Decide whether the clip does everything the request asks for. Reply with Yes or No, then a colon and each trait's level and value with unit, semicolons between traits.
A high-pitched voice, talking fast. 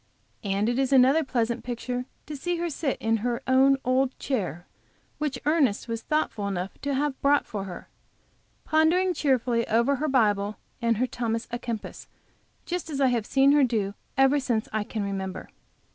No: very high, 250 Hz; average, 175 wpm